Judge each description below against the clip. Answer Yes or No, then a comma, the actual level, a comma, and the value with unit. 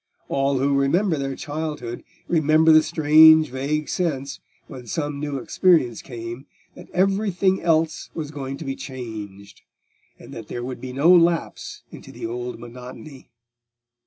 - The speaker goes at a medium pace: Yes, average, 145 wpm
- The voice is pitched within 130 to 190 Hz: Yes, medium, 140 Hz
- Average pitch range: Yes, average, 4.0 semitones